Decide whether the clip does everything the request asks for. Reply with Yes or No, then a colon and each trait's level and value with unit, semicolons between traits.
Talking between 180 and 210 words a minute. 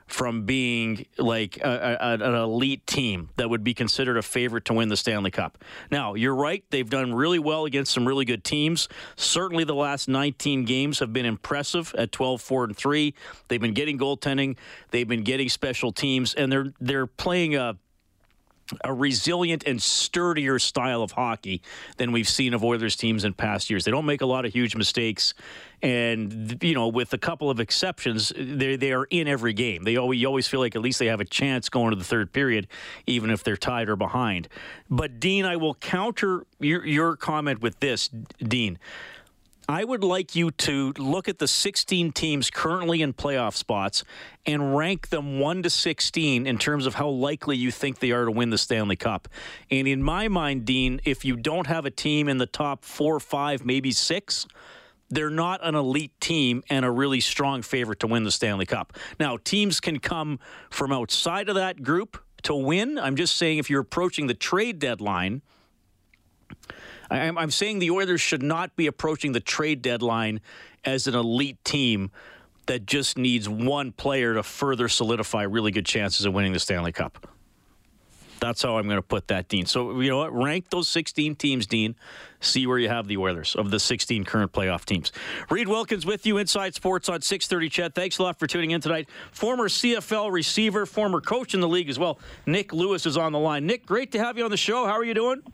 Yes: average, 200 wpm